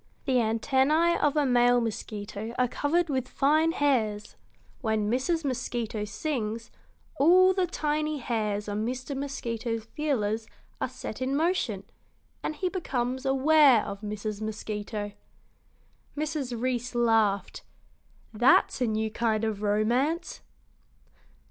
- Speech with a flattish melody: No, average, 4.9 semitones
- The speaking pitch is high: Yes, high, 245 Hz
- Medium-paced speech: No, slow, 120 wpm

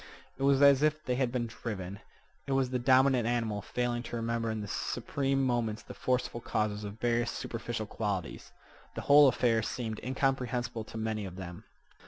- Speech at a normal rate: Yes, average, 180 wpm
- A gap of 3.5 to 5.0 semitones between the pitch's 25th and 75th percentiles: No, average, 2.9 semitones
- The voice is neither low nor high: No, low, 120 Hz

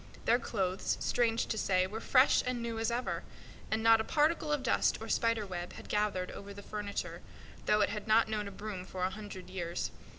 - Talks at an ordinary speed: No, fast, 210 wpm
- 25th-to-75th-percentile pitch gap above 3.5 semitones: No, average, 3.0 semitones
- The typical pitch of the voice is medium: No, high, 215 Hz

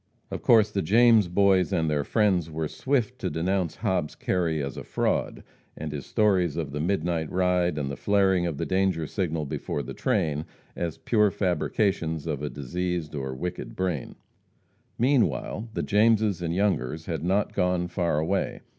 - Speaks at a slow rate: No, average, 170 wpm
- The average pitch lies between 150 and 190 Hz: No, very low, 90 Hz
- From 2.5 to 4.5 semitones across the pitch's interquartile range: Yes, average, 4.0 semitones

